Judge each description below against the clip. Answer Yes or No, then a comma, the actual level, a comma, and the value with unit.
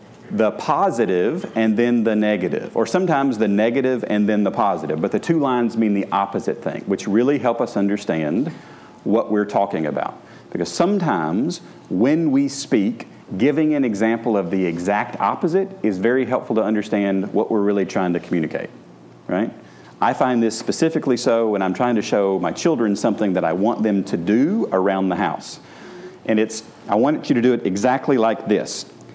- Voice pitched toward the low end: Yes, low, 110 Hz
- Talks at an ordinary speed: Yes, average, 180 wpm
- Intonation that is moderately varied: Yes, average, 4.2 semitones